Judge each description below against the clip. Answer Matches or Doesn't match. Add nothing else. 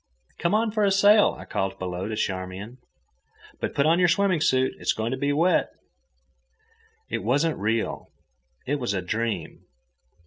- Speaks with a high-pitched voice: Doesn't match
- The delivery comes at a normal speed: Matches